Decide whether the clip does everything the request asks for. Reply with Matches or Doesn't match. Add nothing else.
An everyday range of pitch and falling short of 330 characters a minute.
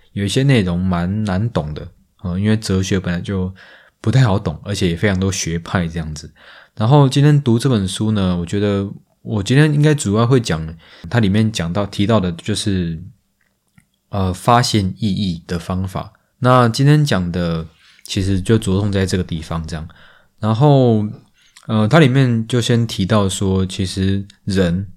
Matches